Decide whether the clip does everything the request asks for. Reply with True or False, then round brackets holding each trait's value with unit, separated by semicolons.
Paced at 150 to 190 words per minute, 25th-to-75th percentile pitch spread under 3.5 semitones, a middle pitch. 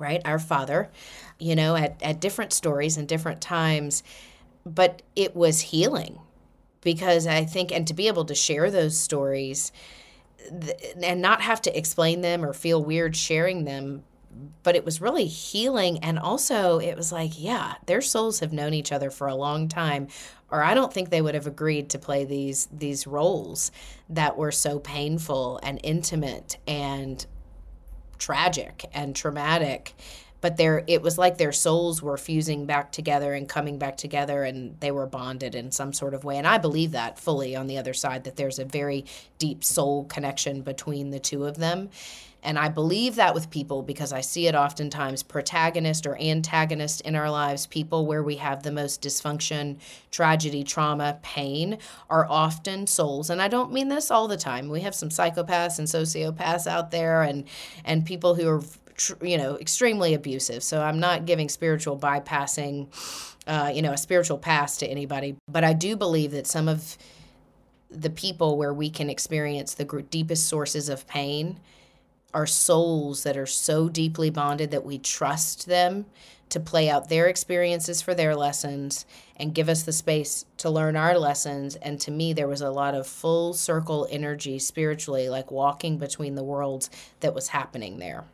True (180 wpm; 2.8 semitones; 155 Hz)